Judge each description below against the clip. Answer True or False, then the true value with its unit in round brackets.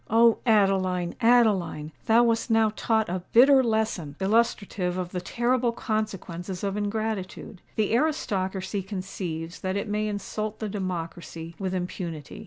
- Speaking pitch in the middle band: False (200 Hz)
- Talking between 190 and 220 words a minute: False (135 wpm)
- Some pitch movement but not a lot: True (3.5 semitones)